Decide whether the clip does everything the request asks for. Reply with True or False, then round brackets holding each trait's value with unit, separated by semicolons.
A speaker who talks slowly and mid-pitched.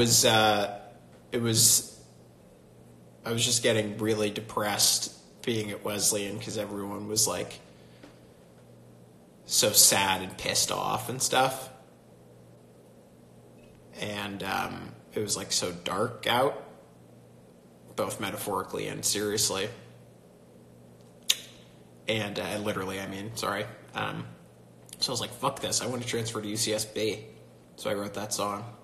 False (125 wpm; 95 Hz)